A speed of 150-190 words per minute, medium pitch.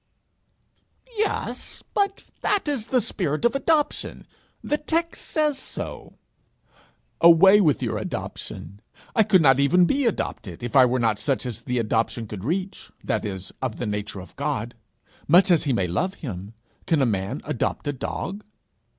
Yes: average, 160 wpm; medium, 150 Hz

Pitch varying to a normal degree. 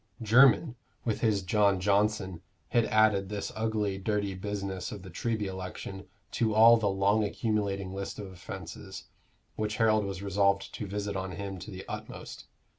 No: narrow, 2.0 semitones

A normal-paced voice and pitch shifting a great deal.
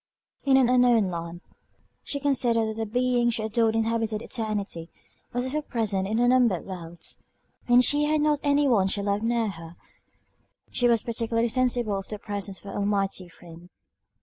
No: average, 170 wpm; average, 3.7 semitones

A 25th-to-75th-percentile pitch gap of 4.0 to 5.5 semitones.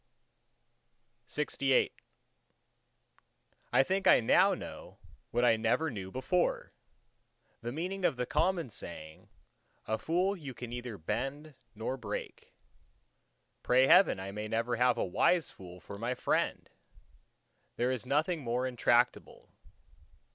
Yes: average, 5.0 semitones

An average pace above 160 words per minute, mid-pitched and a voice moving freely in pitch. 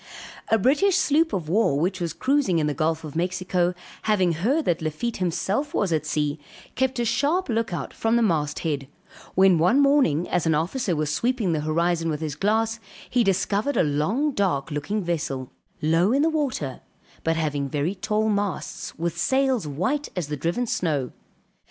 Yes: average, 180 wpm; medium, 180 Hz; wide, 6.8 semitones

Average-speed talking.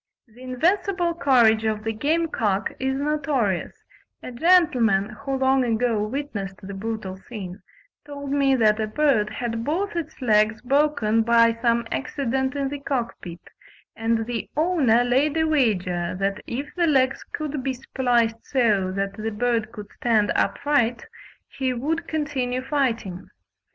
Yes: average, 145 wpm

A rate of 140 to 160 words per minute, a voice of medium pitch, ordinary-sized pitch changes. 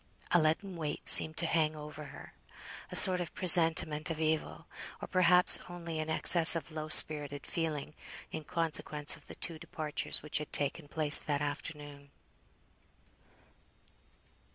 No: average, 145 wpm; medium, 155 Hz; narrow, 1.8 semitones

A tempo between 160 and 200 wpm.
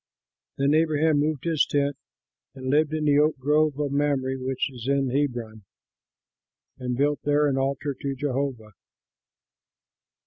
No: average, 140 wpm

